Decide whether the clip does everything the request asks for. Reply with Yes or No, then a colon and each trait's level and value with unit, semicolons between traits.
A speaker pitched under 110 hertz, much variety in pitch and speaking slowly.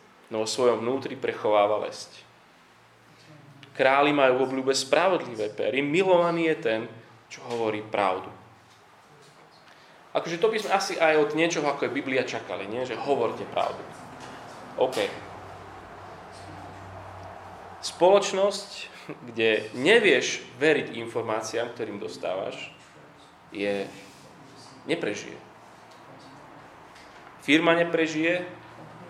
No: low, 135 Hz; wide, 7.3 semitones; slow, 95 wpm